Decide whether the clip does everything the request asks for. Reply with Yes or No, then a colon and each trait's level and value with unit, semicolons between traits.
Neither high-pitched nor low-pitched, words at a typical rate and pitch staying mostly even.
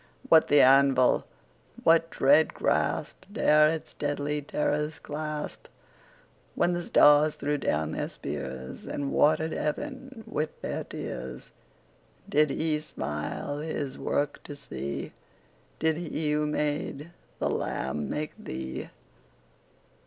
No: medium, 150 Hz; slow, 120 wpm; narrow, 2.2 semitones